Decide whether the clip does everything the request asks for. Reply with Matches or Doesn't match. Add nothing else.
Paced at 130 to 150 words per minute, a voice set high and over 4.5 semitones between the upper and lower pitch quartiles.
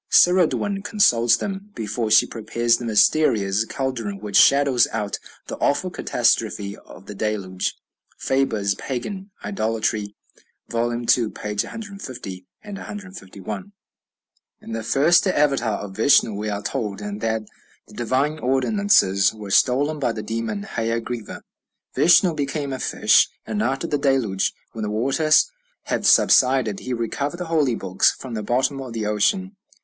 Doesn't match